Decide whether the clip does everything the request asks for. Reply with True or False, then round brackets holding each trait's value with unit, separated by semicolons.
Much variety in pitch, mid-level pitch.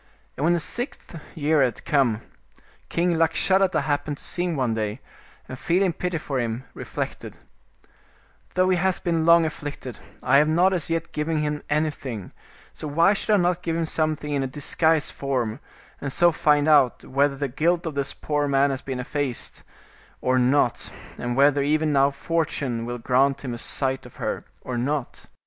False (3.8 semitones; 145 Hz)